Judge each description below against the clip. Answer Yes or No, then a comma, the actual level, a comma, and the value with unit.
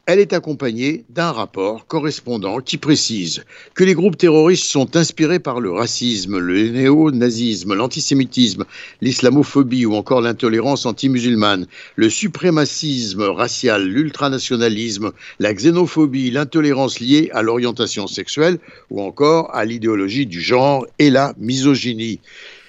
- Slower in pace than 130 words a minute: Yes, average, 120 wpm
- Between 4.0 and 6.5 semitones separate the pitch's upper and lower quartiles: Yes, average, 4.7 semitones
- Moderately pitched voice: No, low, 130 Hz